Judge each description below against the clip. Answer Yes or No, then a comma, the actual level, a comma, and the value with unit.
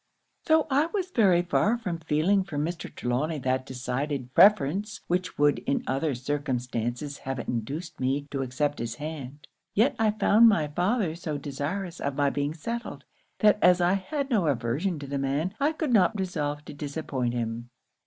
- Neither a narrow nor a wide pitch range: No, wide, 6.2 semitones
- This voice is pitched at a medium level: Yes, medium, 150 Hz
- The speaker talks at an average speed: Yes, average, 175 wpm